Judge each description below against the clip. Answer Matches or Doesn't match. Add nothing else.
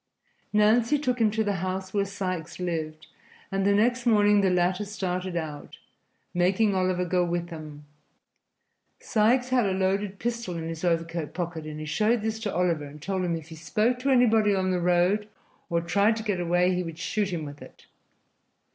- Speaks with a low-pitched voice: Doesn't match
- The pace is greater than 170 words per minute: Matches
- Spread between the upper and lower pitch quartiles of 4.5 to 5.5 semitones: Doesn't match